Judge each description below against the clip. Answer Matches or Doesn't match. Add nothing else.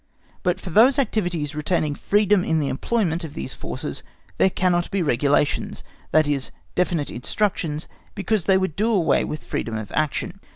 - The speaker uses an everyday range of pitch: Matches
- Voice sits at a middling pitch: Matches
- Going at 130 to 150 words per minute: Doesn't match